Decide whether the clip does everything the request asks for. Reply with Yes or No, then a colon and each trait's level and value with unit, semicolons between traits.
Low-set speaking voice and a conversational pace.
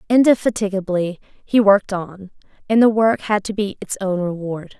No: high, 200 Hz; average, 165 wpm